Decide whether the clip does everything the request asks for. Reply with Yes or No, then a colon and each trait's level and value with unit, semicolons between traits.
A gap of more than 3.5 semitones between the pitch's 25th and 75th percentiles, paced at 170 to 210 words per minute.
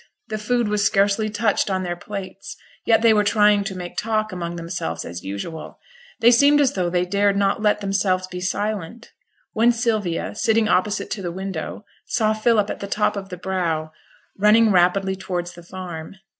No: average, 3.1 semitones; average, 185 wpm